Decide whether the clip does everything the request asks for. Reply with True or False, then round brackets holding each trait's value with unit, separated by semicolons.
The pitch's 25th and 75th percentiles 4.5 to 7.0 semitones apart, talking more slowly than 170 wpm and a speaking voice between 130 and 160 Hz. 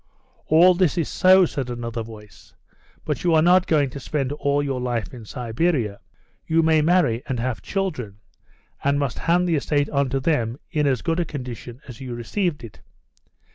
False (5.3 semitones; 185 wpm; 140 Hz)